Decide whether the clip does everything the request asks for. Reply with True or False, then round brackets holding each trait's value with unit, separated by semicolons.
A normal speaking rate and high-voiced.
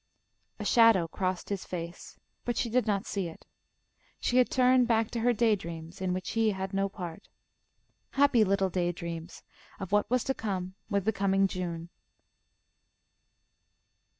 True (160 wpm; 195 Hz)